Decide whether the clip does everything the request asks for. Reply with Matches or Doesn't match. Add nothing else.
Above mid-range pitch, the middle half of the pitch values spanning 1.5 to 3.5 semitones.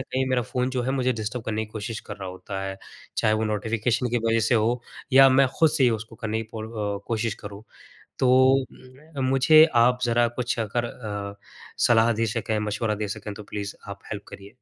Doesn't match